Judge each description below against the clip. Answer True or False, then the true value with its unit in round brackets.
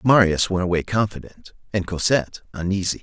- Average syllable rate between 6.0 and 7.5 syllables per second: False (5.7 syllables/s)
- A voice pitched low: True (95 Hz)